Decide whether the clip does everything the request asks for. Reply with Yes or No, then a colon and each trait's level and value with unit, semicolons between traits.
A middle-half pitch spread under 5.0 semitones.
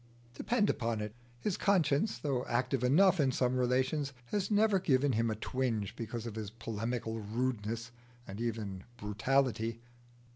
Yes: average, 3.7 semitones